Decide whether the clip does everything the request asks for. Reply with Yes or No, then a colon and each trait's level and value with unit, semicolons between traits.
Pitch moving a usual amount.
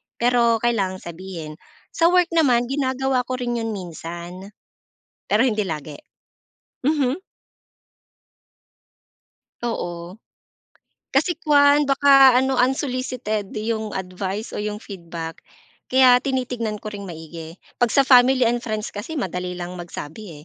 No: wide, 6.0 semitones